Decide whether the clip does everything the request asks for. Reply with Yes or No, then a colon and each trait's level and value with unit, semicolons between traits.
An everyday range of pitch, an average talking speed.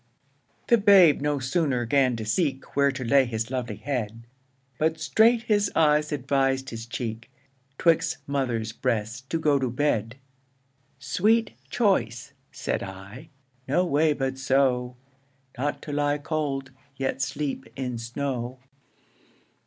No: average, 3.7 semitones; slow, 130 wpm